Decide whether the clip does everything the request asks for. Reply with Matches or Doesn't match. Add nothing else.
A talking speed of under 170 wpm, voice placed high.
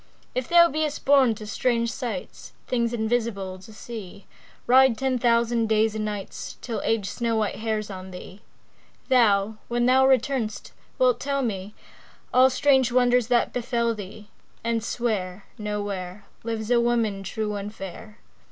Matches